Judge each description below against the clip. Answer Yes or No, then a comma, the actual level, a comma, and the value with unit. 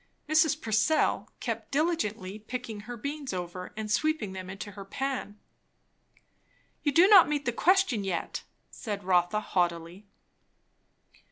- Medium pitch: No, high, 215 Hz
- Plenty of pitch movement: Yes, wide, 7.3 semitones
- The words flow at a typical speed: No, slow, 125 wpm